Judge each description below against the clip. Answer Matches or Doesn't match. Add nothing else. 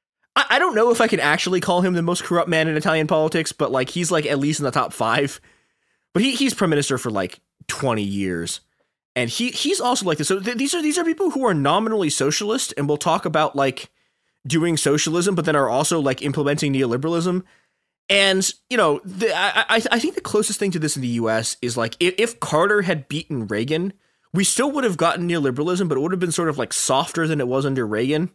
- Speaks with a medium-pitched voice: Matches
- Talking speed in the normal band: Doesn't match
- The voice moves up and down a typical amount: Doesn't match